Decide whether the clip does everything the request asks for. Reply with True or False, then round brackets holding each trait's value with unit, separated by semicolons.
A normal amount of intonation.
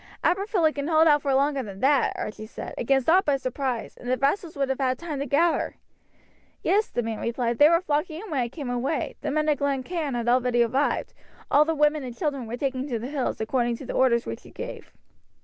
True (3.7 semitones)